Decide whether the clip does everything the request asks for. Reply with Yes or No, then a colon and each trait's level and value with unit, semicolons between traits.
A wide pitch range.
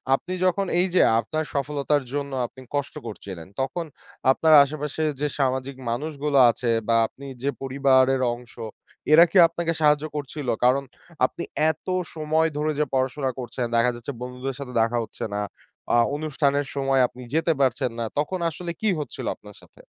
No: average, 3.2 semitones